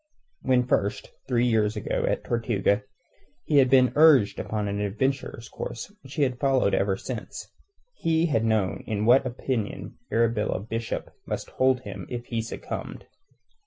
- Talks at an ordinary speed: Yes, average, 155 wpm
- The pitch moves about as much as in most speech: Yes, average, 3.7 semitones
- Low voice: Yes, low, 120 Hz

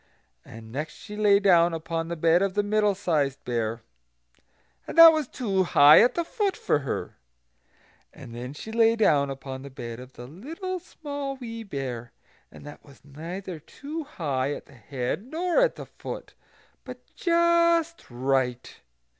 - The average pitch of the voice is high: No, medium, 170 Hz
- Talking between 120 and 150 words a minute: No, average, 165 wpm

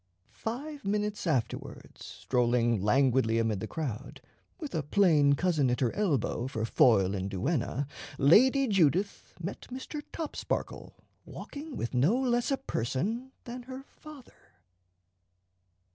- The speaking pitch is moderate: Yes, medium, 160 Hz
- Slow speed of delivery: Yes, slow, 125 wpm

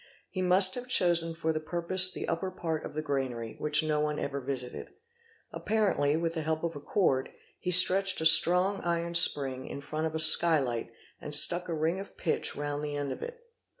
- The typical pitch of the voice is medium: Yes, medium, 160 Hz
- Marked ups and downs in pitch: No, average, 3.5 semitones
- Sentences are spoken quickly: Yes, fast, 210 wpm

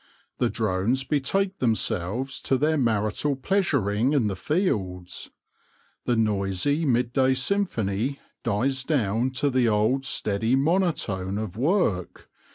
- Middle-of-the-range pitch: No, low, 125 Hz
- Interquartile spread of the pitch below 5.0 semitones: No, wide, 5.4 semitones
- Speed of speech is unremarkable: No, slow, 115 wpm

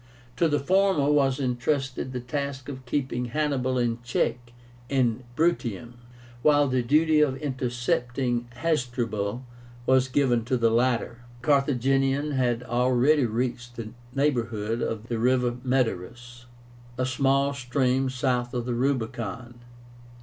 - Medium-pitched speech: No, low, 125 Hz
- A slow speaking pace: Yes, slow, 130 wpm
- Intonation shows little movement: Yes, narrow, 2.2 semitones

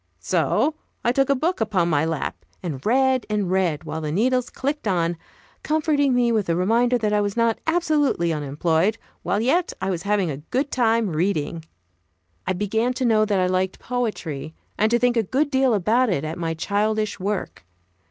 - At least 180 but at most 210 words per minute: Yes, average, 190 wpm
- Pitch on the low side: No, high, 215 Hz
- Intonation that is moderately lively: No, wide, 6.1 semitones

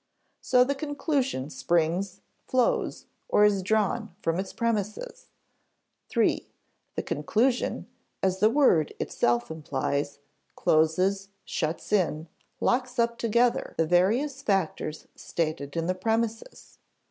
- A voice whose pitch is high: Yes, high, 195 Hz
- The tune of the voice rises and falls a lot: Yes, wide, 6.5 semitones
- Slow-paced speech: Yes, slow, 110 wpm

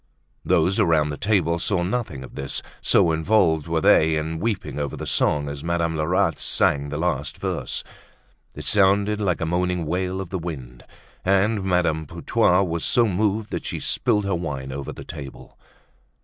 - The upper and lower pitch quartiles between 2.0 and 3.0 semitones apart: No, average, 4.0 semitones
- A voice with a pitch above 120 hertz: No, very low, 85 Hz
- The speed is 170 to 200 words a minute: Yes, average, 175 wpm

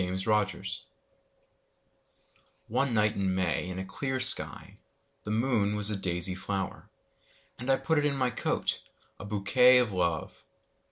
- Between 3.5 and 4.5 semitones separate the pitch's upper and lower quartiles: No, average, 5.0 semitones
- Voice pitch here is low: Yes, low, 105 Hz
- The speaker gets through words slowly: Yes, slow, 125 wpm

